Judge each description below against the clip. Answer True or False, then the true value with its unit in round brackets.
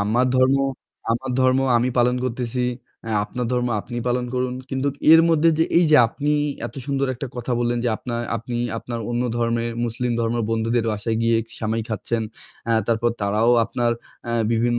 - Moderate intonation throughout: False (1.7 semitones)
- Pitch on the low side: True (120 Hz)